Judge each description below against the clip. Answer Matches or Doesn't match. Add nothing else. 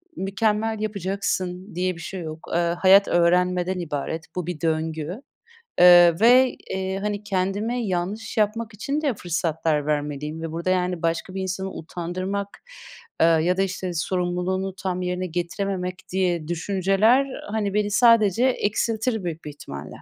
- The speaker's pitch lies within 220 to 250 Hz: Doesn't match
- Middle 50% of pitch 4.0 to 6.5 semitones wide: Doesn't match